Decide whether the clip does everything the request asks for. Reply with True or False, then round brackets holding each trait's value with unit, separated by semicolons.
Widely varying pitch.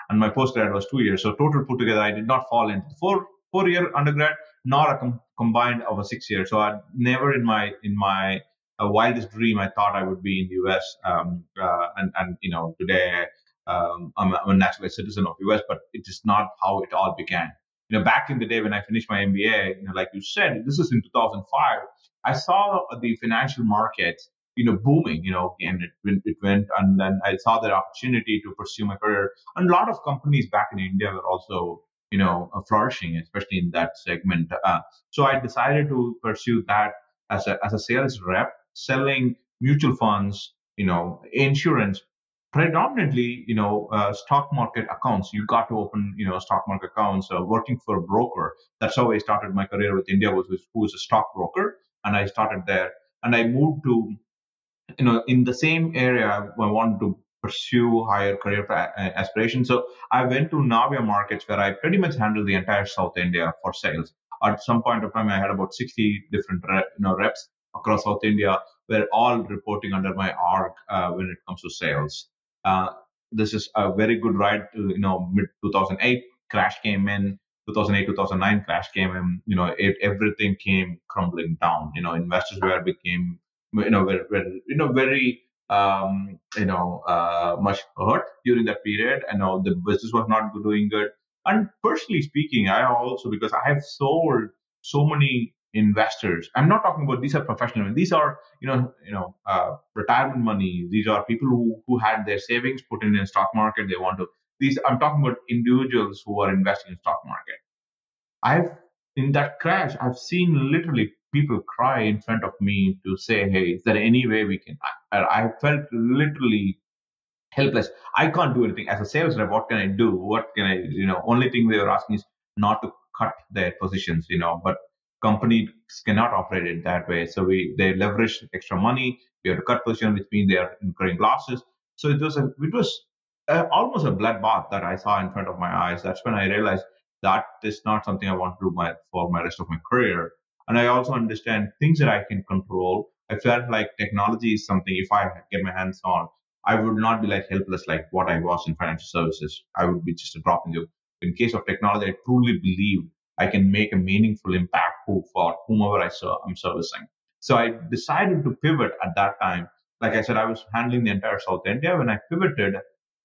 False (4.2 semitones)